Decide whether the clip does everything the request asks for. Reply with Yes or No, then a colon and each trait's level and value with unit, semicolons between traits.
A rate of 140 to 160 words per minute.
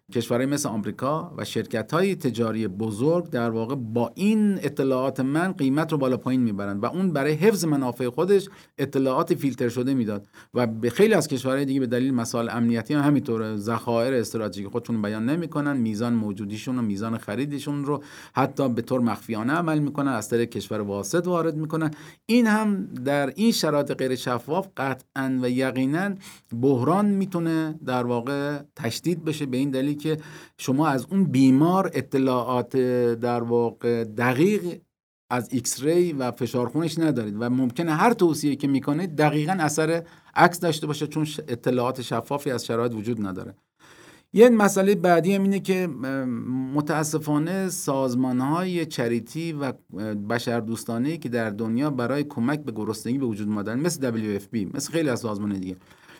Yes: fast, 155 wpm